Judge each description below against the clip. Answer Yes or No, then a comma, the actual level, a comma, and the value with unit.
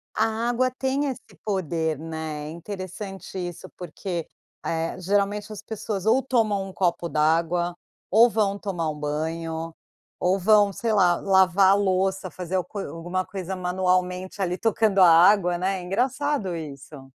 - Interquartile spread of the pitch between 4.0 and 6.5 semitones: No, average, 3.3 semitones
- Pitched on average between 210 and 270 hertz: No, medium, 185 Hz